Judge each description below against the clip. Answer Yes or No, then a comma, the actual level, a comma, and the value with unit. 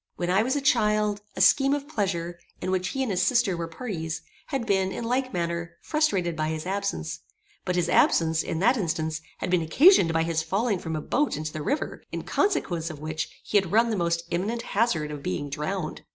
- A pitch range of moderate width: No, wide, 6.0 semitones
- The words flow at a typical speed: No, fast, 215 wpm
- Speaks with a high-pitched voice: No, medium, 180 Hz